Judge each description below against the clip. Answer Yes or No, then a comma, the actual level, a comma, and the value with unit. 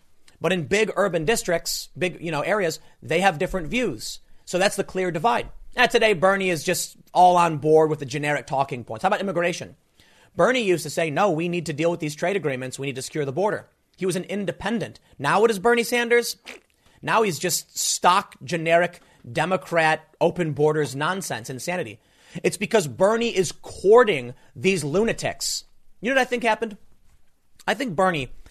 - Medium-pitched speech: Yes, medium, 175 Hz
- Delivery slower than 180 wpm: No, average, 185 wpm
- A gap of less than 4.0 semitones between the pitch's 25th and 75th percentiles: No, average, 4.4 semitones